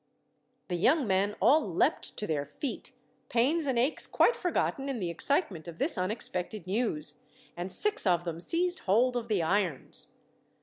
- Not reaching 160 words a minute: No, average, 165 wpm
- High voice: Yes, high, 210 Hz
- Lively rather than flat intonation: Yes, wide, 7.5 semitones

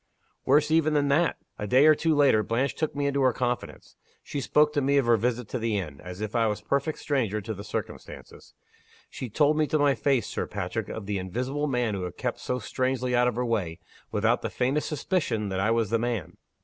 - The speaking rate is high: Yes, fast, 235 wpm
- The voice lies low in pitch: Yes, low, 125 Hz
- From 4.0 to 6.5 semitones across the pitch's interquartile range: Yes, average, 4.9 semitones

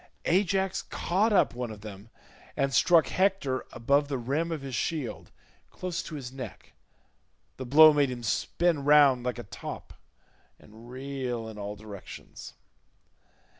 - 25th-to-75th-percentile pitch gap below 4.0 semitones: No, average, 4.9 semitones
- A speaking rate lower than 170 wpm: Yes, average, 145 wpm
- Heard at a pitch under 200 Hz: Yes, low, 135 Hz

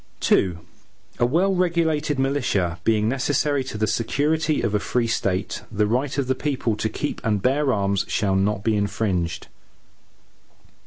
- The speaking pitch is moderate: No, low, 115 Hz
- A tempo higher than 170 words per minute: No, average, 155 wpm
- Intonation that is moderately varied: No, wide, 5.8 semitones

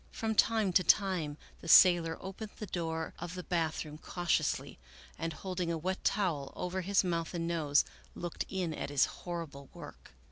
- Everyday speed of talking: Yes, average, 170 wpm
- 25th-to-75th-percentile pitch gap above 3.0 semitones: No, narrow, 2.5 semitones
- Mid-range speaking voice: Yes, medium, 170 Hz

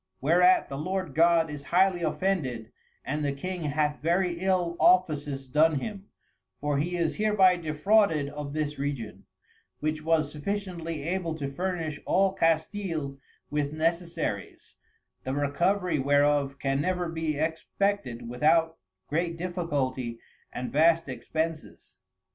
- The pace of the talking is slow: Yes, slow, 125 wpm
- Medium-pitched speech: Yes, medium, 160 Hz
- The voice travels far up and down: No, average, 3.7 semitones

